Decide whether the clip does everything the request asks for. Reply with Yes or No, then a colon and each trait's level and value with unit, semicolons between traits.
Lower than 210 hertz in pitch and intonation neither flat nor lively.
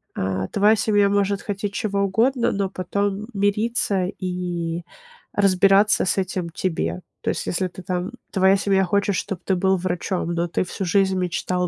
No: high, 190 Hz; narrow, 2.0 semitones